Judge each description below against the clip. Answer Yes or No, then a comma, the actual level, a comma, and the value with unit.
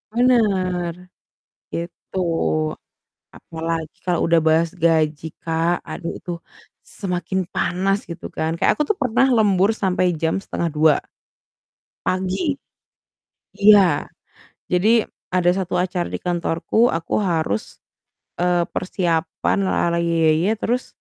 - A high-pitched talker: No, medium, 180 Hz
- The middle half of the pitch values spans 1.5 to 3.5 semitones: Yes, average, 2.8 semitones